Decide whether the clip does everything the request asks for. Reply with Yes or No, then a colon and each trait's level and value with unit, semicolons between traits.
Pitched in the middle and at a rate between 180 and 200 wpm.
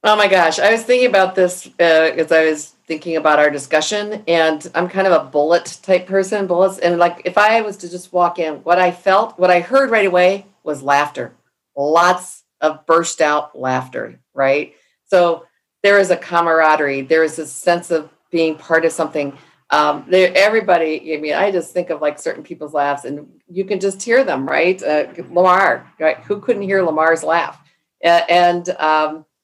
Yes: medium, 170 Hz; average, 190 wpm